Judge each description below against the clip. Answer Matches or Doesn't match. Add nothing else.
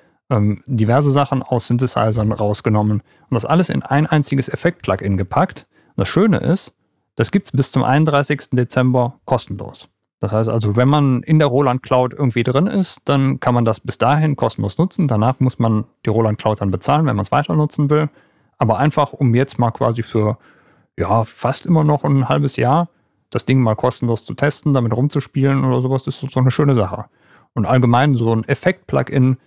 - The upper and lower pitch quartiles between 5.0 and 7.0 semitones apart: Doesn't match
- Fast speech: Matches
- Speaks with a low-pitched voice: Matches